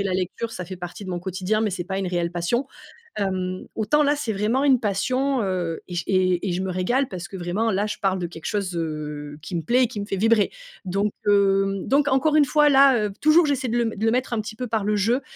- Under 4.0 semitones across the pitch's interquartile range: No, average, 4.6 semitones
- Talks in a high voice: Yes, high, 200 Hz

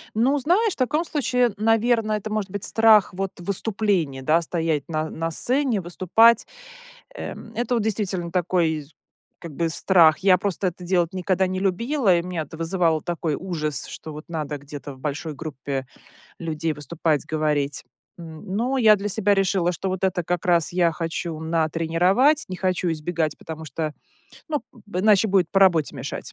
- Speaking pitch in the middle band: Yes, medium, 180 Hz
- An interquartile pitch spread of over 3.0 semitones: Yes, average, 4.5 semitones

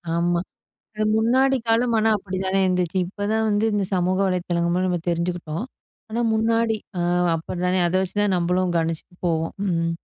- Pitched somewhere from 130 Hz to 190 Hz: Yes, medium, 185 Hz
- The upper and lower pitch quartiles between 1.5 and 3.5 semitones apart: No, average, 4.0 semitones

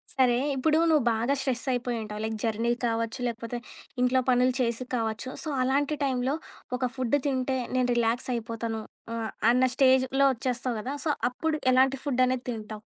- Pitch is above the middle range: Yes, very high, 250 Hz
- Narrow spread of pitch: Yes, narrow, 2.2 semitones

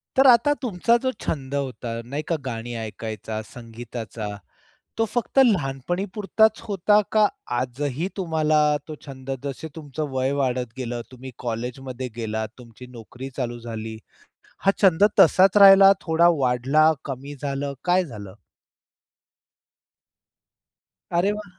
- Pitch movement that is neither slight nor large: No, wide, 6.9 semitones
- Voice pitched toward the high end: No, low, 135 Hz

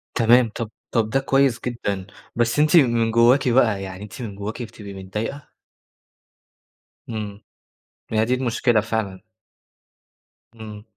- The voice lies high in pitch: No, low, 115 Hz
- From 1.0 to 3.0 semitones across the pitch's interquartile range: Yes, average, 2.7 semitones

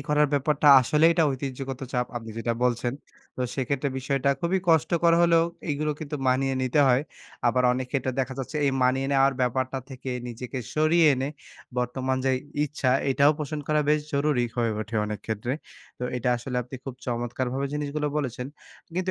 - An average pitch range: Yes, average, 3.0 semitones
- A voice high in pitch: No, low, 135 Hz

